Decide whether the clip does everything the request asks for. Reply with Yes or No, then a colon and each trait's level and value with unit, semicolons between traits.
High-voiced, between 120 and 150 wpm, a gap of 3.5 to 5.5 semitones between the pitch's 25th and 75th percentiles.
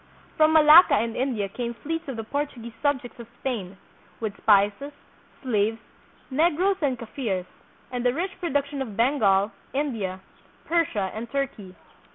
Yes: high, 245 Hz; average, 140 wpm; average, 5.2 semitones